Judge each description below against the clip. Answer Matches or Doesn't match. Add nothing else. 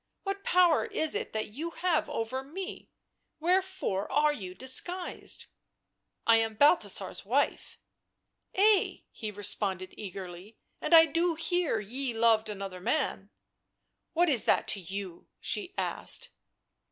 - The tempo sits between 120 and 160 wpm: Matches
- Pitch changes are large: Matches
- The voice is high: Matches